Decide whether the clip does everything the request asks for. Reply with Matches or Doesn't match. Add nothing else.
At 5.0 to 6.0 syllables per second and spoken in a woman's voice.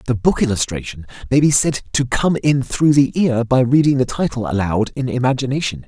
Doesn't match